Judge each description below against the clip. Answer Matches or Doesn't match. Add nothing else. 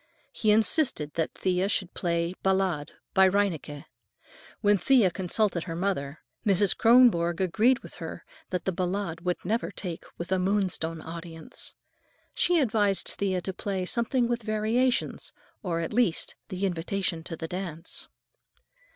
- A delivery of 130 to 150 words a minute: Matches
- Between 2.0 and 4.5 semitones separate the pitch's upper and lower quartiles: Matches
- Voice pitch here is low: Doesn't match